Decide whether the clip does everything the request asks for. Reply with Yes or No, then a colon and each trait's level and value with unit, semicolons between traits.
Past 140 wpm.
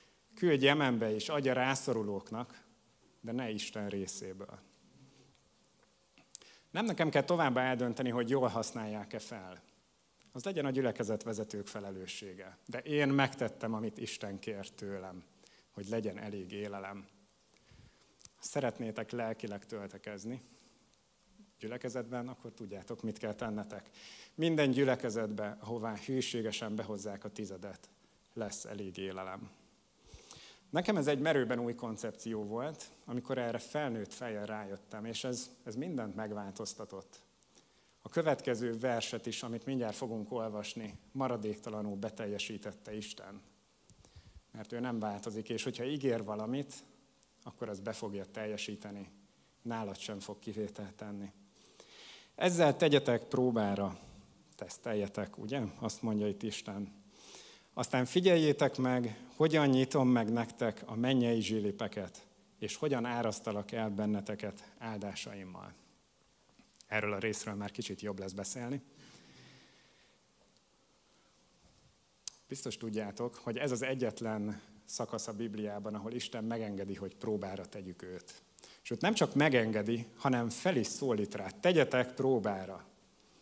No: average, 115 wpm